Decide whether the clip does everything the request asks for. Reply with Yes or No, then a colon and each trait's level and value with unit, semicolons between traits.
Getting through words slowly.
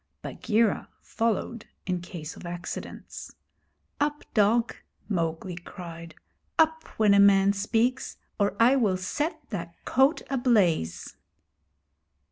Yes: slow, 105 wpm